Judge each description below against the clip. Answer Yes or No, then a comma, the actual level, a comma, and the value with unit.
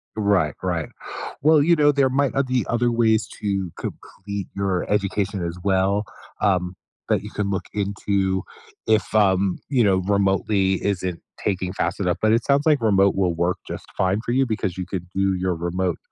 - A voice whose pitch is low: Yes, low, 100 Hz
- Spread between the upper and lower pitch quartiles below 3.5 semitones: Yes, average, 2.9 semitones